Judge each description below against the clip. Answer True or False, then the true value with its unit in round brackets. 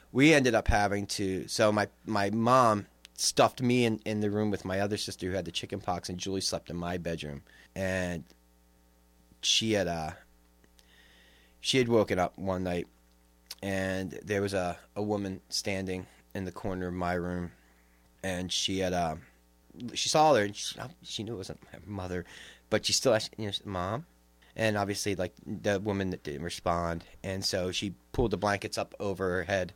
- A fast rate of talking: False (185 wpm)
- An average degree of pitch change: False (5.7 semitones)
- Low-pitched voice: True (90 Hz)